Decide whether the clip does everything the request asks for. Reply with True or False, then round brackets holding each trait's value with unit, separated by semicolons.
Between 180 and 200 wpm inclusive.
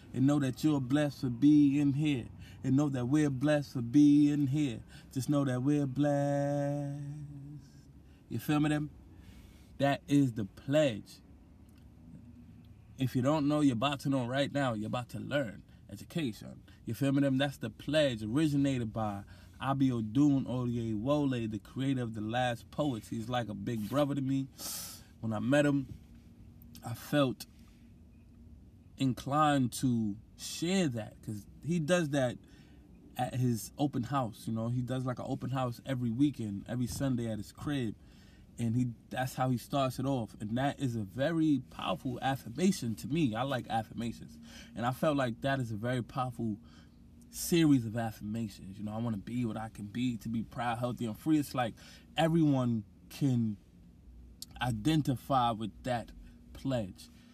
False (165 wpm)